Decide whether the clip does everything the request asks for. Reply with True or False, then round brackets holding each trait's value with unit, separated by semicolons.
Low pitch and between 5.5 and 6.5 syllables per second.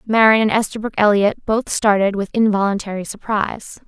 False (210 Hz; 5.6 syllables/s)